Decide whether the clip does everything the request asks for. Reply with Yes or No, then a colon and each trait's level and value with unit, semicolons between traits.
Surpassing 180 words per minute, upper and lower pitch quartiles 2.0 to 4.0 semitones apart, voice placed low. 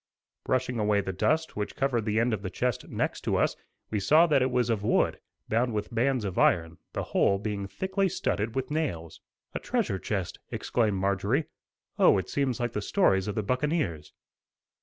No: average, 190 wpm; average, 4.8 semitones; low, 110 Hz